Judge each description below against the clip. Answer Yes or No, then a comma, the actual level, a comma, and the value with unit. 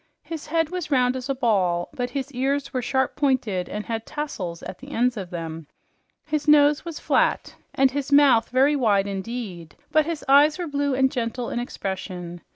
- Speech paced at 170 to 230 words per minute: Yes, average, 190 wpm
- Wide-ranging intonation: Yes, wide, 6.0 semitones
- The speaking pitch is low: No, very high, 255 Hz